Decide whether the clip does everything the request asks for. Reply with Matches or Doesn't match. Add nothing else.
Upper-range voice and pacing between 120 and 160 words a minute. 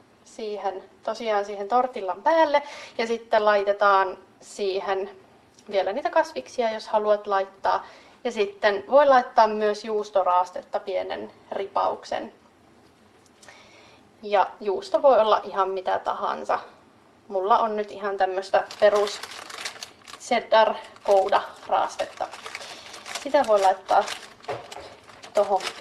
Doesn't match